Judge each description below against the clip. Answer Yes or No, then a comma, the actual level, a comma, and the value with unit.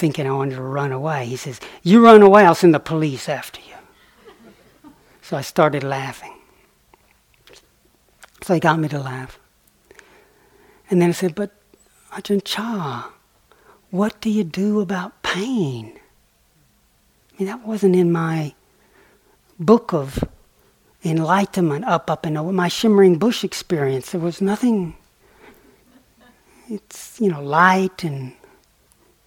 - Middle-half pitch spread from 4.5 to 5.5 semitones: Yes, average, 5.2 semitones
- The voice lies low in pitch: No, medium, 175 Hz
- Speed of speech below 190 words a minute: Yes, slow, 135 wpm